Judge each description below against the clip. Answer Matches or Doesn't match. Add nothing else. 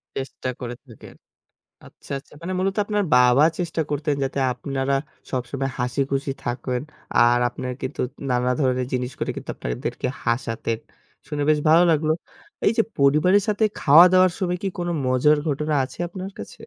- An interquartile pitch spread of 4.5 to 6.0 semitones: Matches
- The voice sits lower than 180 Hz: Matches